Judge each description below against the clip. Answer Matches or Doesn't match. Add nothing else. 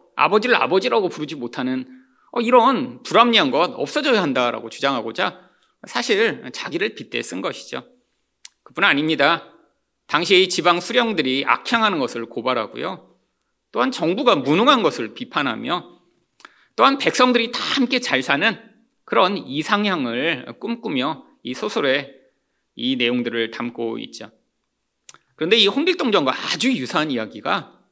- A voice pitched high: Matches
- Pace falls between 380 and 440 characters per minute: Doesn't match